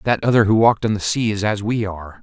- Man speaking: Yes, male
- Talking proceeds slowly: No, fast, 295 wpm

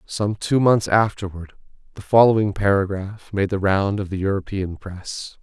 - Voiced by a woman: No, male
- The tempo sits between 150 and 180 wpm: Yes, average, 155 wpm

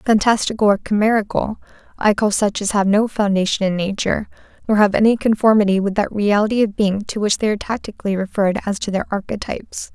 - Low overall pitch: No, high, 205 Hz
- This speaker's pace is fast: No, average, 185 wpm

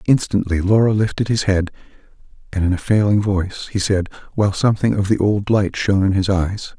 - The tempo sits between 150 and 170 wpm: No, average, 195 wpm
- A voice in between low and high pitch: No, low, 100 Hz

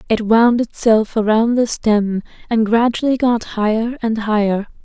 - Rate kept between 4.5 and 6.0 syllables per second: No, 4.0 syllables/s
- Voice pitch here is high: Yes, high, 225 Hz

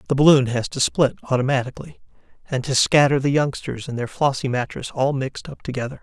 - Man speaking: Yes, male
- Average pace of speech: Yes, average, 190 wpm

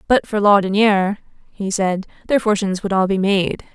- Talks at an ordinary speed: Yes, average, 175 wpm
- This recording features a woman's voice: Yes, female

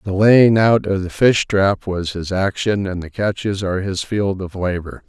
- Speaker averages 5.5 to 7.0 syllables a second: No, 4.4 syllables/s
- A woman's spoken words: No, male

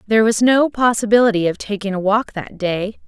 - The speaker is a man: No, female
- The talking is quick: No, average, 195 wpm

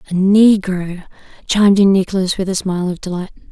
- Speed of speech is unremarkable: Yes, average, 170 wpm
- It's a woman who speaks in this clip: Yes, female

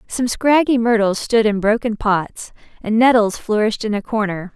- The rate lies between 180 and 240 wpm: No, average, 170 wpm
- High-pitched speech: Yes, high, 220 Hz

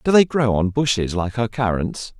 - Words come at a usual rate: No, fast, 220 wpm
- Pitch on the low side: Yes, low, 115 Hz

